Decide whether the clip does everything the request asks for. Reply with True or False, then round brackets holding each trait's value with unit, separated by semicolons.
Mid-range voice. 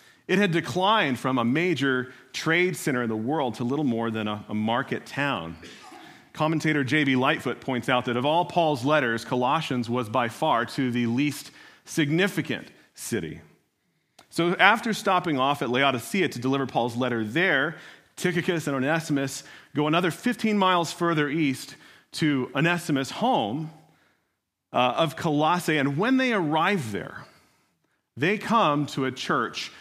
True (150 Hz)